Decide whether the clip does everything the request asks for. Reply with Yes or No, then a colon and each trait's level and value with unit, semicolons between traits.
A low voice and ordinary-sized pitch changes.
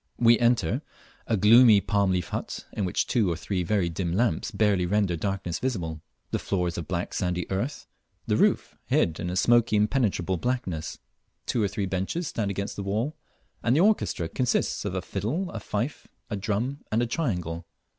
Yes: low, 100 Hz; average, 4.8 semitones